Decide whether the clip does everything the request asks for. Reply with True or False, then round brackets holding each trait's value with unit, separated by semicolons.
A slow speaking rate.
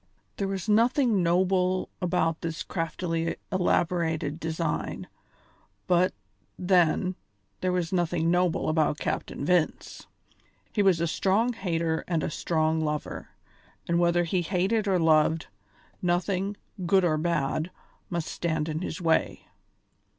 True (125 wpm)